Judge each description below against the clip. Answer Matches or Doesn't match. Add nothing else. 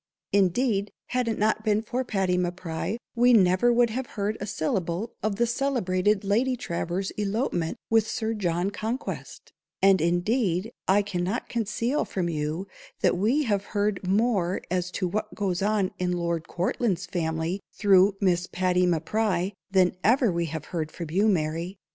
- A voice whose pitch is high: Matches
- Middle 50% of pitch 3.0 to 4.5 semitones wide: Matches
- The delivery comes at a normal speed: Matches